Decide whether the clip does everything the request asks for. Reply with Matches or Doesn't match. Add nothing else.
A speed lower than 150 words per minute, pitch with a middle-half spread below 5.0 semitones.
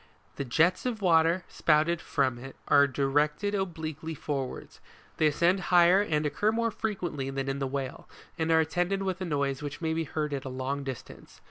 Doesn't match